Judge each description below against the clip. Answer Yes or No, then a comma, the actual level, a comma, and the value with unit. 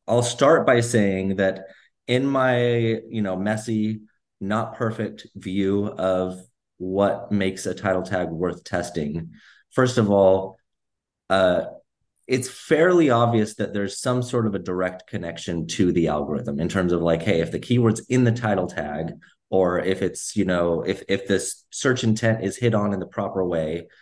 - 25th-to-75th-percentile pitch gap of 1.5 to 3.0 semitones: No, average, 3.7 semitones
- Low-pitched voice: Yes, low, 100 Hz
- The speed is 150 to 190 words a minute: Yes, average, 170 wpm